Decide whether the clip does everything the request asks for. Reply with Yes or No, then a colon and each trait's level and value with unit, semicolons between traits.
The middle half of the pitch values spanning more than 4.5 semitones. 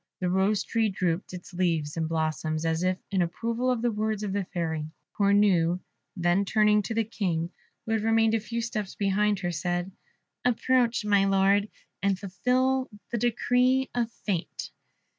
No: average, 4.2 semitones